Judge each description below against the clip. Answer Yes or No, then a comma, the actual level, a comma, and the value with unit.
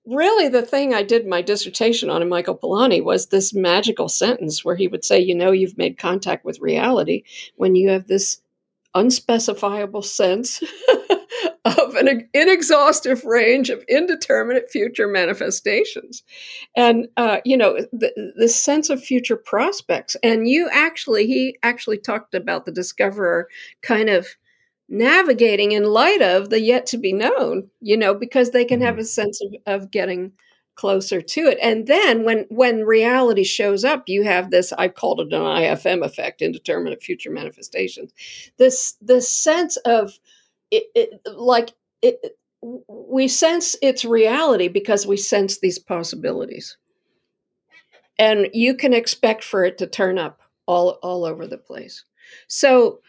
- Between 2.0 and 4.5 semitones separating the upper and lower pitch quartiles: No, wide, 5.4 semitones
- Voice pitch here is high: Yes, high, 230 Hz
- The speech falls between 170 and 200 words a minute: No, average, 155 wpm